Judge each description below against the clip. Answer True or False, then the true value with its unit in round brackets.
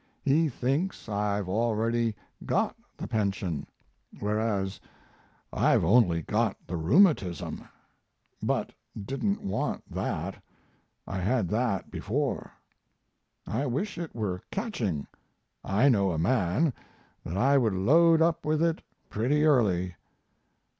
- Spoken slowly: True (115 wpm)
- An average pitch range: False (6.9 semitones)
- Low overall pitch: True (115 Hz)